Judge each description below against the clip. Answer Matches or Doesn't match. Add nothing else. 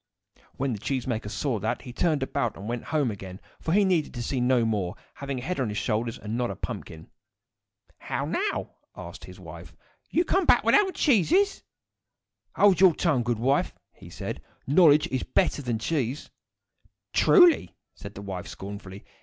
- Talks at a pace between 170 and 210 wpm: Matches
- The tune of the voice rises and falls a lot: Matches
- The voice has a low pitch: Matches